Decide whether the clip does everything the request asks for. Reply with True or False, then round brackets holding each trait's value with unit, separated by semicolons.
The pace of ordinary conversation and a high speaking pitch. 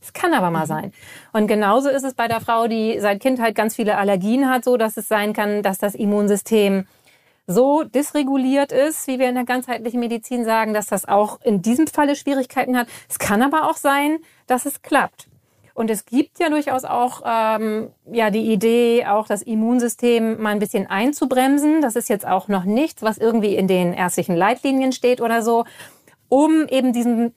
False (195 wpm; 235 Hz)